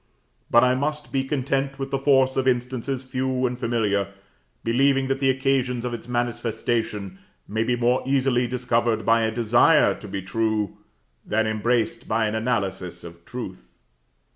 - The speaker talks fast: No, average, 160 wpm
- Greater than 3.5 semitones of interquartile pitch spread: No, average, 3.0 semitones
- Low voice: Yes, low, 120 Hz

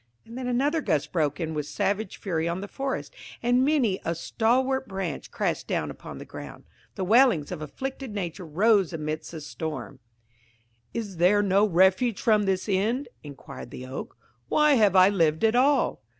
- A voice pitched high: Yes, high, 195 Hz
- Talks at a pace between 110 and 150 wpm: No, average, 175 wpm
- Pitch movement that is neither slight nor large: No, wide, 6.6 semitones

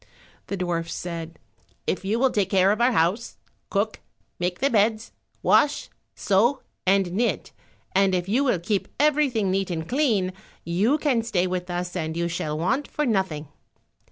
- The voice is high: Yes, high, 195 Hz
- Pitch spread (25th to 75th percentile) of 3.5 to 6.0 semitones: Yes, average, 4.8 semitones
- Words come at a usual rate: Yes, average, 165 wpm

